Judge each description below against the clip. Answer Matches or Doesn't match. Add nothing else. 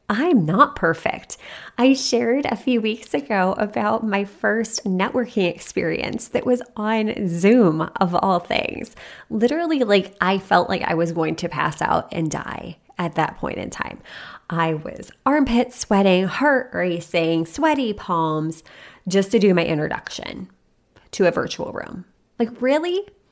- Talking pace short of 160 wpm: Matches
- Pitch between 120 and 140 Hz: Doesn't match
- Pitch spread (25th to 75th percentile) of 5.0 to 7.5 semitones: Matches